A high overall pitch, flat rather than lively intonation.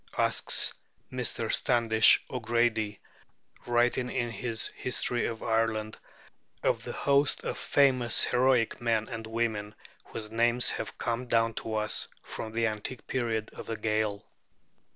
No: low, 115 Hz; narrow, 1.6 semitones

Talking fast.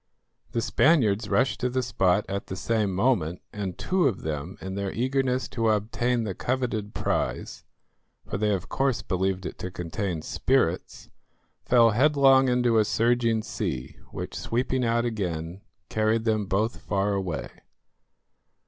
No: average, 150 wpm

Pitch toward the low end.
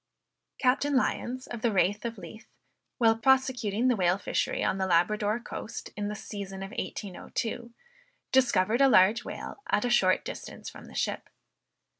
No: high, 220 Hz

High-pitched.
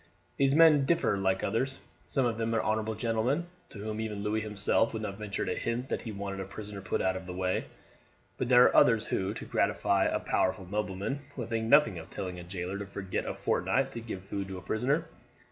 No: low, 110 Hz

